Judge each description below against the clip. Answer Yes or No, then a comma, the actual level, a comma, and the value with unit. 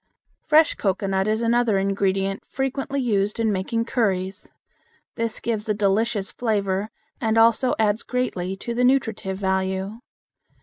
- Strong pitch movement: No, average, 3.2 semitones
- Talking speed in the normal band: No, slow, 130 wpm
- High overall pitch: Yes, high, 215 Hz